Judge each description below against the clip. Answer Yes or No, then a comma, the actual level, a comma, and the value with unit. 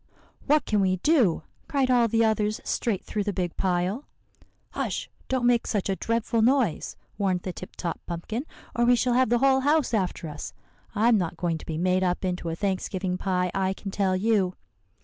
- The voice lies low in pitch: No, high, 200 Hz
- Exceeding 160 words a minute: Yes, average, 195 wpm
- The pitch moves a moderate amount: Yes, average, 4.6 semitones